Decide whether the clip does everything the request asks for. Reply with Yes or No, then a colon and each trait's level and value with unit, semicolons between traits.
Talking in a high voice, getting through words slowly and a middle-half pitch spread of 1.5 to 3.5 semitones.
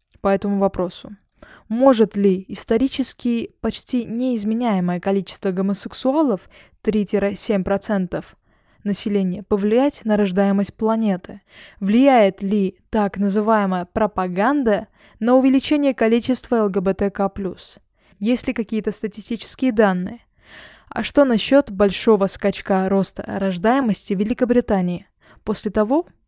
Yes: high, 210 Hz; slow, 95 wpm; average, 3.1 semitones